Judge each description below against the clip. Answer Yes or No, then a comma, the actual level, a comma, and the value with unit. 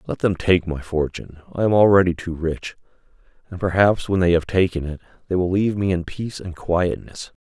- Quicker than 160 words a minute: Yes, average, 200 wpm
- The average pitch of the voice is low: Yes, very low, 90 Hz